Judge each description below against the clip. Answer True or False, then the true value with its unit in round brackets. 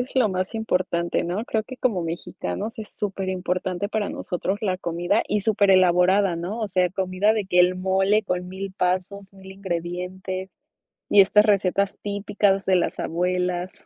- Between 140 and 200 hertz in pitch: True (190 Hz)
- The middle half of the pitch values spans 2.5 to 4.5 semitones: False (2.0 semitones)